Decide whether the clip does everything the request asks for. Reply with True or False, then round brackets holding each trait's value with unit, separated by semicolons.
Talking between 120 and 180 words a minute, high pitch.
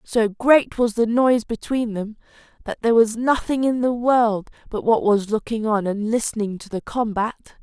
False (190 wpm; 225 Hz)